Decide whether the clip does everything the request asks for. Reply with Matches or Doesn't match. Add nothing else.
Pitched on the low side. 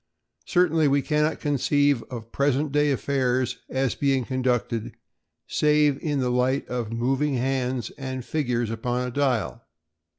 Matches